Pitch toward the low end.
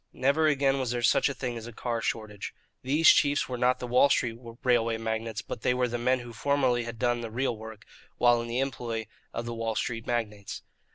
Yes: low, 120 Hz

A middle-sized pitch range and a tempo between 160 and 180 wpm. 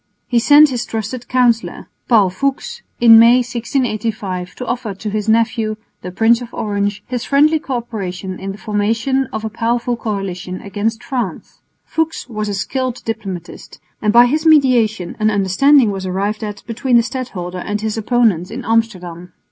Yes: average, 3.4 semitones; average, 165 wpm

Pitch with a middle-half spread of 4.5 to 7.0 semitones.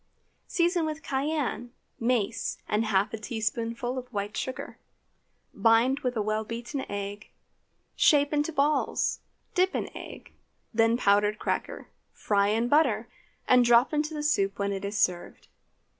Yes: average, 5.1 semitones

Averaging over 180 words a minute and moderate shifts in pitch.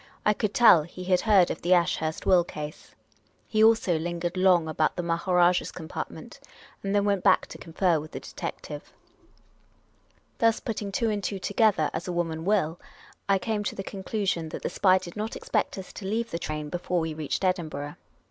Yes: average, 195 wpm; average, 3.6 semitones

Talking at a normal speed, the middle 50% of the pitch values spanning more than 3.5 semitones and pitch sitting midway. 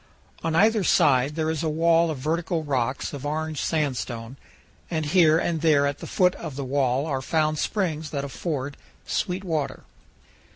No: average, 170 wpm; average, 2.7 semitones; medium, 155 Hz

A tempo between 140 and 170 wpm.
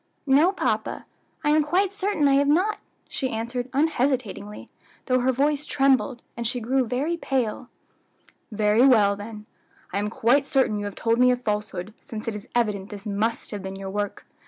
No: average, 180 wpm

